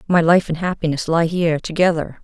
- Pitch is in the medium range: Yes, medium, 165 Hz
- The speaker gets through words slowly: No, average, 190 wpm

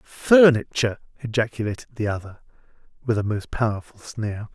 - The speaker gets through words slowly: Yes, slow, 120 wpm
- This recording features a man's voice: Yes, male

